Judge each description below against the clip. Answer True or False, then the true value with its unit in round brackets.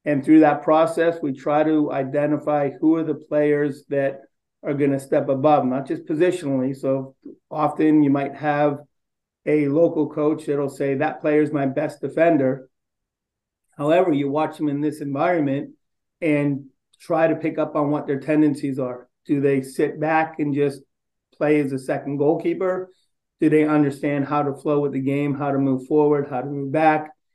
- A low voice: False (145 Hz)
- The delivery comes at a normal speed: True (180 wpm)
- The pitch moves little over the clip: True (1.7 semitones)